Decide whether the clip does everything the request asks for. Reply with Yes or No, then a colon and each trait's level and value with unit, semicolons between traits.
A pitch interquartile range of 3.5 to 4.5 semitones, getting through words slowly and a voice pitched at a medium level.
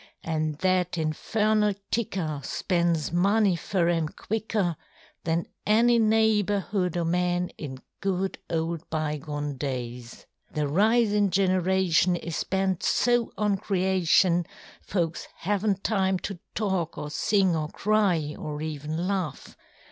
Yes: average, 4.0 semitones; slow, 115 wpm; medium, 180 Hz